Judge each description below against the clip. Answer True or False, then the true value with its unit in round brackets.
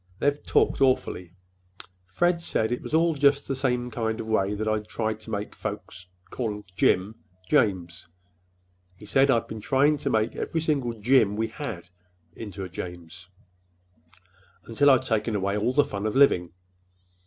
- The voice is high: False (110 Hz)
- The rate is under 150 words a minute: False (165 wpm)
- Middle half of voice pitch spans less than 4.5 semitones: False (5.1 semitones)